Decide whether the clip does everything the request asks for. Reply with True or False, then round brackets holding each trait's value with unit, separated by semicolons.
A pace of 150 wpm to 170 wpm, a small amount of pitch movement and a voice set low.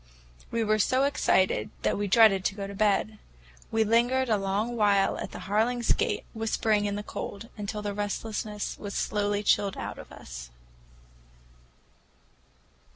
False (155 wpm; 1.7 semitones; 210 Hz)